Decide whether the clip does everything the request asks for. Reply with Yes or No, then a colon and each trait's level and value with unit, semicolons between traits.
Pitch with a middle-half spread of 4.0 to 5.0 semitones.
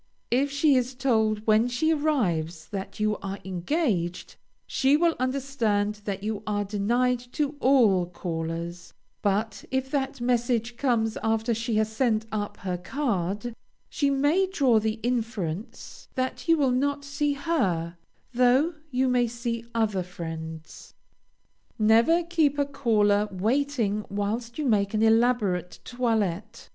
Yes: average, 4.7 semitones